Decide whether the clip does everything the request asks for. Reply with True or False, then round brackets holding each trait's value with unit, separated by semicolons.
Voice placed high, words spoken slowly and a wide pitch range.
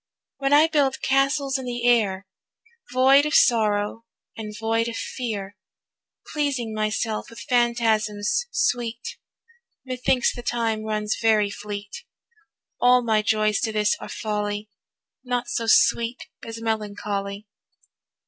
False (225 Hz; 120 wpm; 2.7 semitones)